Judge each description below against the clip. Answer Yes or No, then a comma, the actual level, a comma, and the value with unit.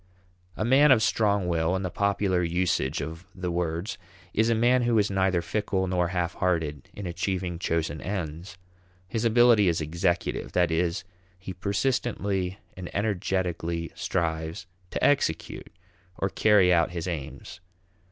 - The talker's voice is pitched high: No, very low, 90 Hz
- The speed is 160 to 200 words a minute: No, average, 145 wpm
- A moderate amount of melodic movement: Yes, average, 3.3 semitones